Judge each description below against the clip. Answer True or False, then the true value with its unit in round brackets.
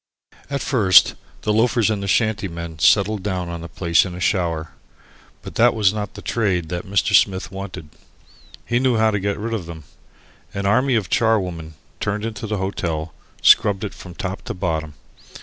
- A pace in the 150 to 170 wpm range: False (185 wpm)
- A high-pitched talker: False (100 Hz)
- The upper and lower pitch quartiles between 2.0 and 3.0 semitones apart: False (3.7 semitones)